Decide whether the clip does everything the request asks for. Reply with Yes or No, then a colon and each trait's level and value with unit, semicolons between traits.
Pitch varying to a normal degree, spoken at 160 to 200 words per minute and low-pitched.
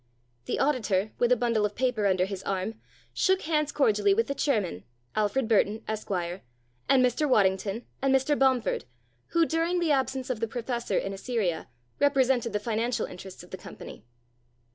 No: average, 4.6 semitones; average, 165 wpm; high, 230 Hz